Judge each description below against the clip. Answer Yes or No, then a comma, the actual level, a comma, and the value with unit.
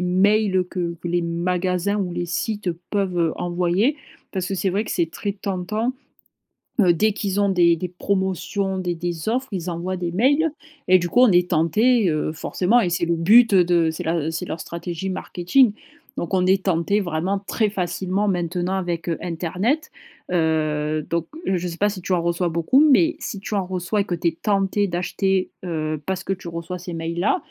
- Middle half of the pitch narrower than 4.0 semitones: Yes, average, 2.7 semitones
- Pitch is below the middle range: No, medium, 180 Hz